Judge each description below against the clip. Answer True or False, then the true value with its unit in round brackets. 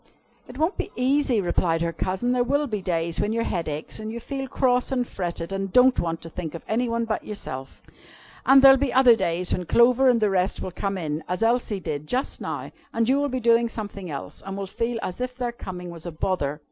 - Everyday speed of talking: False (235 wpm)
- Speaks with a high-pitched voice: True (215 Hz)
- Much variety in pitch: True (5.9 semitones)